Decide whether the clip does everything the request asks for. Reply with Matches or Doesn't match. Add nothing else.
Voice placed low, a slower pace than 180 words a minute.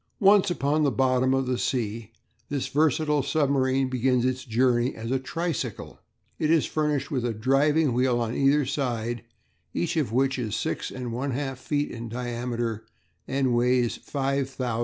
Matches